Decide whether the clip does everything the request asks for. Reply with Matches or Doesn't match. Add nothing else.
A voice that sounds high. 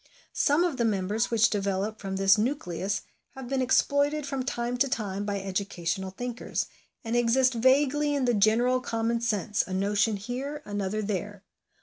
Matches